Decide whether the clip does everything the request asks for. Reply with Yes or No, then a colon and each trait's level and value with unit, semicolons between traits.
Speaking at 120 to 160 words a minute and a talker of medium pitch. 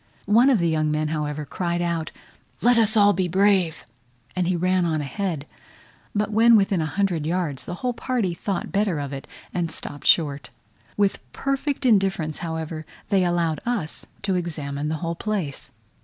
No: average, 170 wpm; medium, 175 Hz